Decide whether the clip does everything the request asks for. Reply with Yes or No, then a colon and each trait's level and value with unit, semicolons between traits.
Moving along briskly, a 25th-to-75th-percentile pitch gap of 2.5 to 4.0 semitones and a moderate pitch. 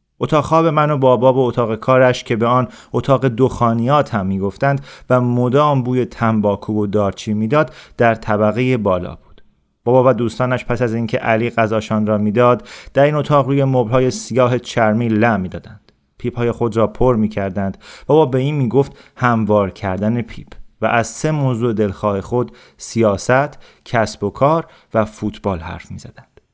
No: fast, 170 wpm; average, 3.3 semitones; low, 120 Hz